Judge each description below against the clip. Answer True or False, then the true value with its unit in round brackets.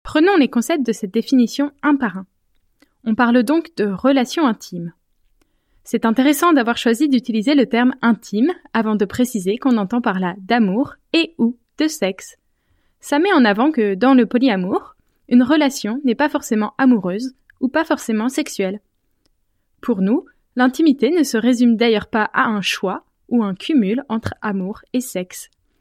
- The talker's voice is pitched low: False (245 Hz)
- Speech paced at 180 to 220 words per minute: False (165 wpm)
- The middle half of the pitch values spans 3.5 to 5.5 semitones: True (4.6 semitones)